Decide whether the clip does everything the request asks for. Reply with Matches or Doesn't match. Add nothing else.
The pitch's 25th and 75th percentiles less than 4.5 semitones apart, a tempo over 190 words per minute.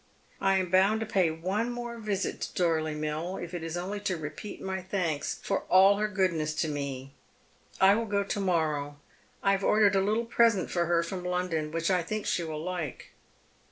Matches